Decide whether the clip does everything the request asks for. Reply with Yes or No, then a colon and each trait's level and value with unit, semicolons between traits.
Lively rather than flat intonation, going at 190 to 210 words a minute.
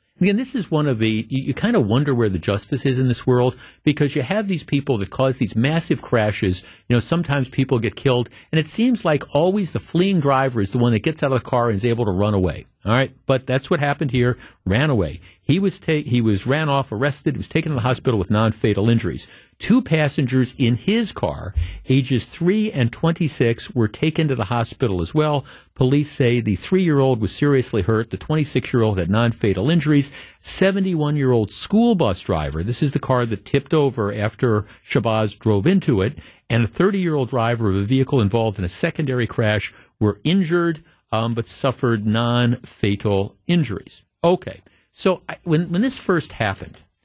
Yes: wide, 5.7 semitones; average, 200 wpm